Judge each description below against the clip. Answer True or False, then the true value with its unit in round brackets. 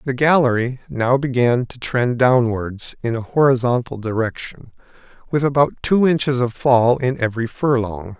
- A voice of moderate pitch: False (125 Hz)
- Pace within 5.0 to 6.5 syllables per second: False (4.7 syllables/s)